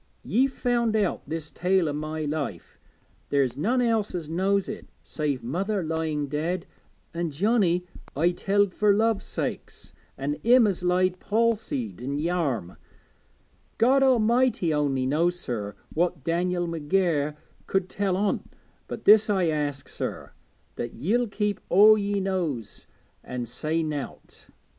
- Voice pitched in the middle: Yes, medium, 175 Hz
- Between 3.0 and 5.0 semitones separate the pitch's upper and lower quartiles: No, wide, 5.5 semitones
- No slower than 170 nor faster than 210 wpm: No, average, 140 wpm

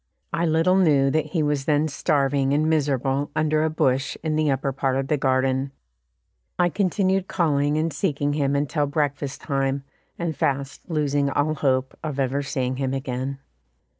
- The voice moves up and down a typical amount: No, narrow, 2.3 semitones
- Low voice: No, medium, 145 Hz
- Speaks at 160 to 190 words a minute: Yes, average, 165 wpm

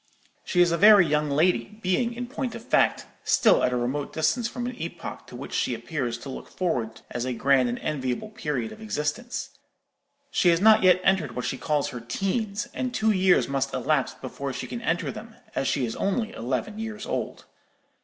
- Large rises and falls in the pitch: Yes, wide, 8.3 semitones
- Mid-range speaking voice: Yes, medium, 170 Hz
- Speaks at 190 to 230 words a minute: Yes, fast, 205 wpm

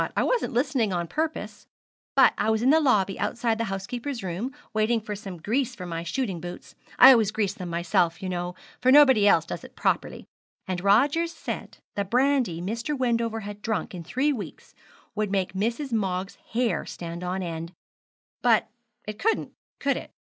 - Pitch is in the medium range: No, high, 215 Hz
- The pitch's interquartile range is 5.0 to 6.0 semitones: Yes, average, 5.3 semitones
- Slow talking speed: No, average, 180 wpm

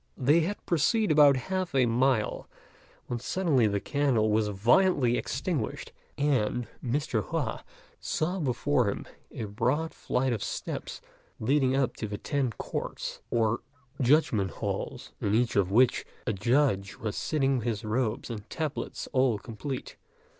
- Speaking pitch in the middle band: No, low, 125 Hz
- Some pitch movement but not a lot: Yes, average, 4.9 semitones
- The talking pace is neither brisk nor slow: Yes, average, 145 wpm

